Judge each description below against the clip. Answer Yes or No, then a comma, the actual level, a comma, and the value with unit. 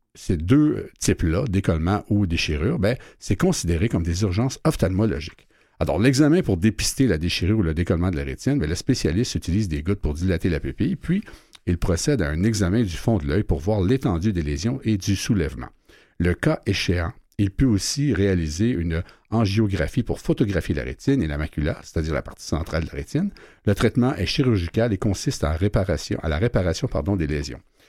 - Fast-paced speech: No, average, 195 wpm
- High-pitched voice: No, very low, 95 Hz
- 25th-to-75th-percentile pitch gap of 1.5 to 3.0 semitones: No, average, 5.3 semitones